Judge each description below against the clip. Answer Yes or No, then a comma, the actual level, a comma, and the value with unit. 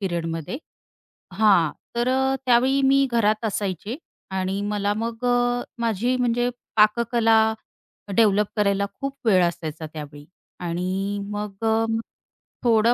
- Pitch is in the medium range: No, high, 215 Hz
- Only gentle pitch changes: No, average, 3.7 semitones